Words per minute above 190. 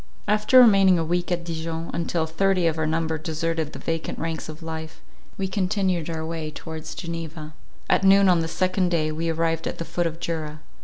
Yes: average, 200 wpm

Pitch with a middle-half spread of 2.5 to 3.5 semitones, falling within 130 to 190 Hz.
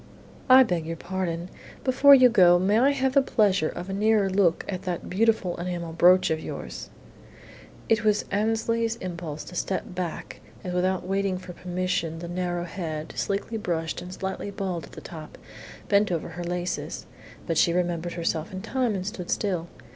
Yes: average, 3.1 semitones; medium, 185 Hz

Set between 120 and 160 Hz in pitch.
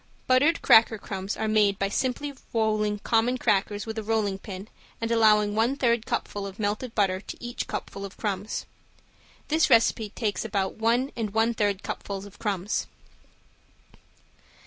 No: high, 215 Hz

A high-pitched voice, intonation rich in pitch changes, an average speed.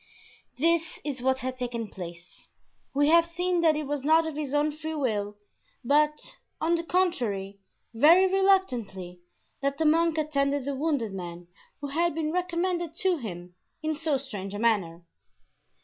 Yes: very high, 290 Hz; wide, 6.4 semitones; average, 160 wpm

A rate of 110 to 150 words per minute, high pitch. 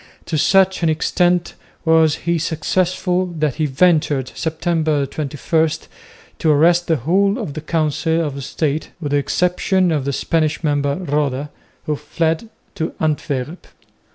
No: average, 140 wpm; medium, 160 Hz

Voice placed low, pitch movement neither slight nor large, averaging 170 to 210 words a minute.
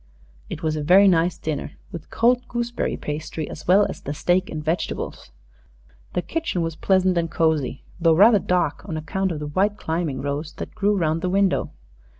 No: medium, 170 Hz; average, 3.7 semitones; average, 185 wpm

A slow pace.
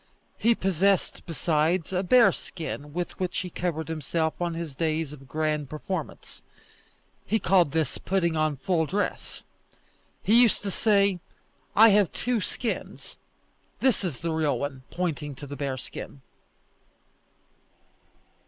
Yes: slow, 130 wpm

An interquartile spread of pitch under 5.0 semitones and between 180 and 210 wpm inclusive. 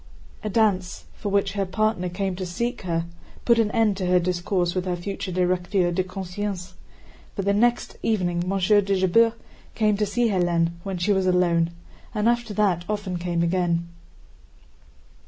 No: average, 2.8 semitones; average, 170 wpm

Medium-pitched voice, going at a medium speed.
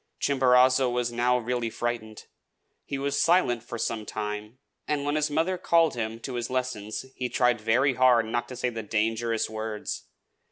No: low, 120 Hz; average, 170 wpm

